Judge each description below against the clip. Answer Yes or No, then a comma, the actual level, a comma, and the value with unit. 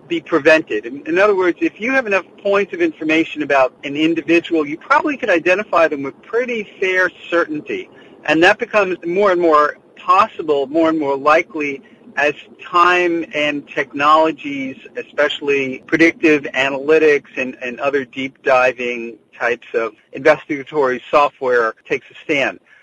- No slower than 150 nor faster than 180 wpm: No, average, 140 wpm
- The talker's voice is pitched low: No, medium, 165 Hz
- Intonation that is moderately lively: No, wide, 5.9 semitones